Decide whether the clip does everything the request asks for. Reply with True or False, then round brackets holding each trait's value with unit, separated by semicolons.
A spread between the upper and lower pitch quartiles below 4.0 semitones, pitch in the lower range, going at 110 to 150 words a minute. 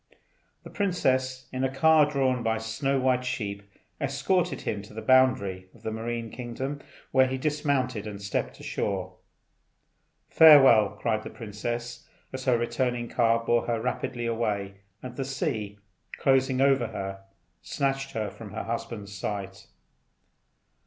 True (3.6 semitones; 120 Hz; 140 wpm)